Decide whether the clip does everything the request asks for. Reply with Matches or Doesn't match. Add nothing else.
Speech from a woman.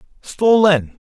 Doesn't match